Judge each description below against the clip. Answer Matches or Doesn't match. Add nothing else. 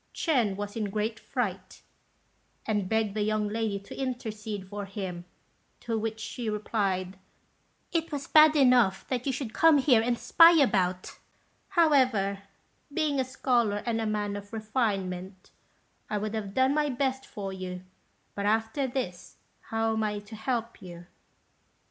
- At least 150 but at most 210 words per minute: Matches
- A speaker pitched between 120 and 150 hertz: Doesn't match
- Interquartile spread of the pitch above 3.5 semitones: Matches